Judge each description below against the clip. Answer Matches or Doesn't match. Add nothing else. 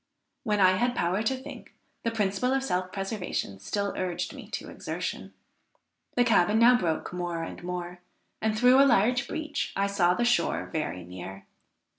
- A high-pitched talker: Matches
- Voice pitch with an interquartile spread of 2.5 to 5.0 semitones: Doesn't match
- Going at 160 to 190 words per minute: Matches